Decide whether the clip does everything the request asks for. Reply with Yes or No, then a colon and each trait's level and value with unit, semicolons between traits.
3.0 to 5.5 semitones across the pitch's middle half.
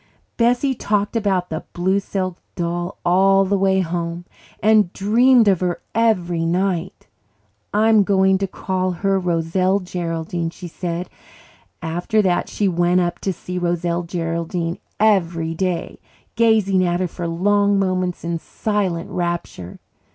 No: narrow, 2.5 semitones